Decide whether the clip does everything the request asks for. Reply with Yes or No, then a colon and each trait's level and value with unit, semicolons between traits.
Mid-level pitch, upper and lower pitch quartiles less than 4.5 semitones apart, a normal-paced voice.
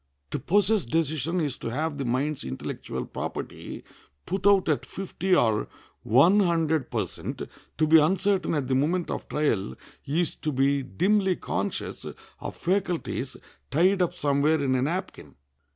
No: medium, 155 Hz; average, 5.1 semitones; average, 150 wpm